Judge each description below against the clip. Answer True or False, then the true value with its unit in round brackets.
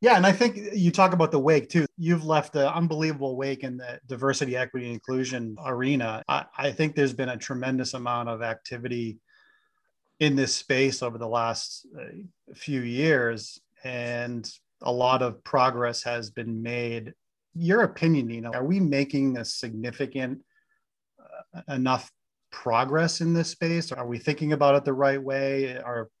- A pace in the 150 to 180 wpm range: True (165 wpm)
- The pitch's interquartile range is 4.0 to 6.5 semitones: True (4.5 semitones)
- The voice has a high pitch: False (135 Hz)